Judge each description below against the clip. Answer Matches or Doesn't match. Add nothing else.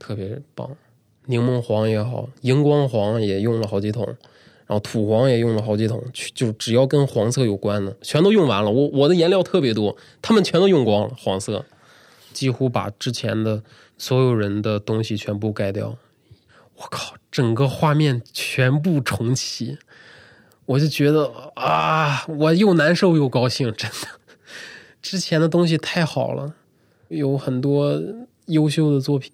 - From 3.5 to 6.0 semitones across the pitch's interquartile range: Matches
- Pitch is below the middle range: Matches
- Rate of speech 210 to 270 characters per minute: Matches